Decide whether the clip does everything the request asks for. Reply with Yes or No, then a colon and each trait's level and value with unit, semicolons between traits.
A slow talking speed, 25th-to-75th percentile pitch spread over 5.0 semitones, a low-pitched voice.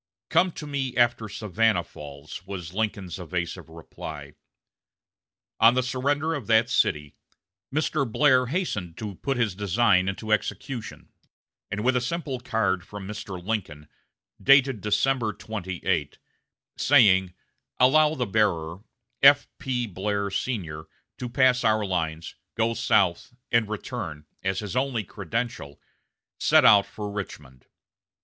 Yes: slow, 125 wpm; wide, 5.6 semitones; low, 105 Hz